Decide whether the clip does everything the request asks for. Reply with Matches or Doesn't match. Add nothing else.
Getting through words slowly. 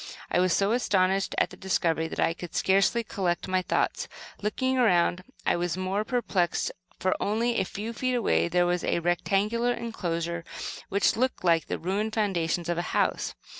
Doesn't match